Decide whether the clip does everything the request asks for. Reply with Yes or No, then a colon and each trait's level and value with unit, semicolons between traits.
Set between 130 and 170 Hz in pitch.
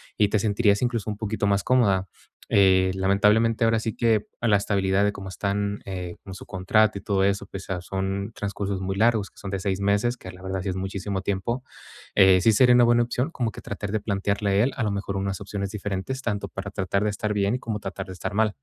No: low, 100 Hz